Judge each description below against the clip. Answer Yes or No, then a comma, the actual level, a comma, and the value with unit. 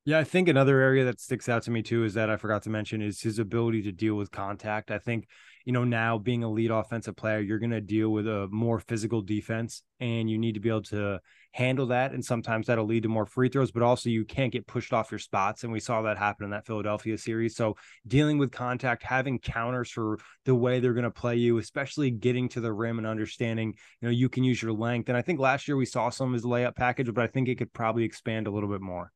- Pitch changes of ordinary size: No, narrow, 2.2 semitones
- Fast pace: Yes, fast, 265 wpm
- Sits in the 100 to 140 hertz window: Yes, low, 115 Hz